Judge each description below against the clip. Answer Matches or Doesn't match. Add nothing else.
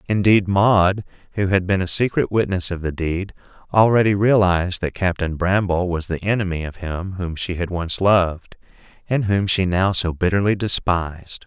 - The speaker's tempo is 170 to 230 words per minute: Matches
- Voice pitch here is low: Matches